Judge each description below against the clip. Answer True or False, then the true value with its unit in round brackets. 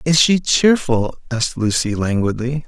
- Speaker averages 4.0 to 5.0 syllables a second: True (4.5 syllables/s)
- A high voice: False (130 Hz)